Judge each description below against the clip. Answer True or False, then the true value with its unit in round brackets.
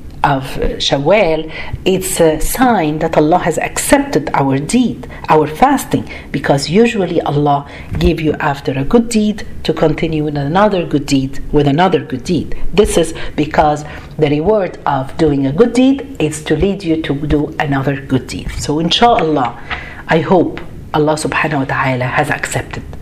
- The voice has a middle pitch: True (155 Hz)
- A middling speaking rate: False (160 wpm)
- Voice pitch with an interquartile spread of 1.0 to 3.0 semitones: False (3.9 semitones)